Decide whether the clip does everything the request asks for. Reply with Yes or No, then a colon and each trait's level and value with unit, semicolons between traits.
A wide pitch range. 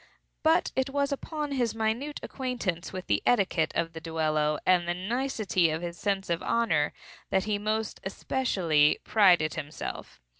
Yes: wide, 6.7 semitones